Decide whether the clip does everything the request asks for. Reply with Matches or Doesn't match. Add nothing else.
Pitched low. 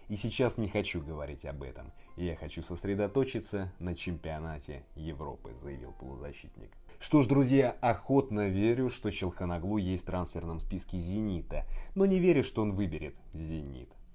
Matches